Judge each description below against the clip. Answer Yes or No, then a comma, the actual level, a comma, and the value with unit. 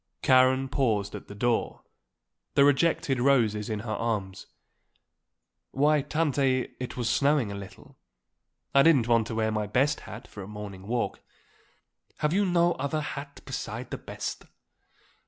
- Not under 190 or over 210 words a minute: No, average, 150 wpm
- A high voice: No, low, 130 Hz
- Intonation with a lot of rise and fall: No, average, 4.7 semitones